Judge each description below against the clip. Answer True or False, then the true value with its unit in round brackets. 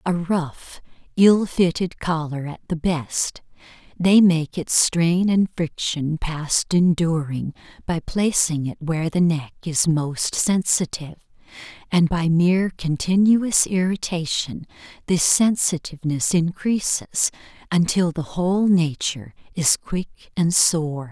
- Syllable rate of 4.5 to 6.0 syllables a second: False (3.8 syllables/s)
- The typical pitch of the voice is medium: True (170 Hz)